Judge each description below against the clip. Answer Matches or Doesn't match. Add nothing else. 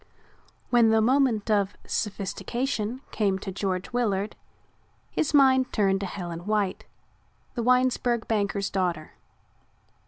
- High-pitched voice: Matches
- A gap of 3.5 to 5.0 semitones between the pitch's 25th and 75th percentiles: Matches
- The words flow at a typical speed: Doesn't match